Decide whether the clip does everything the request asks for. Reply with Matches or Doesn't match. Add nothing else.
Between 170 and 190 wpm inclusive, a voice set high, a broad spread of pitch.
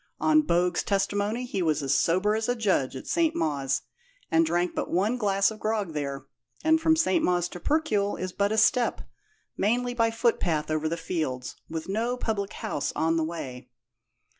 Matches